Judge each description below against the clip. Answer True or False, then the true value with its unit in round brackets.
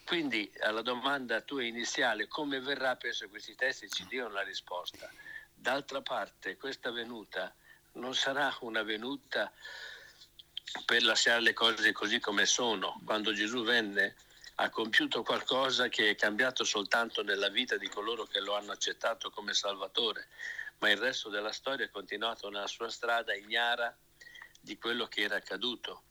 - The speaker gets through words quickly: False (150 wpm)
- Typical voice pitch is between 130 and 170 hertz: True (140 Hz)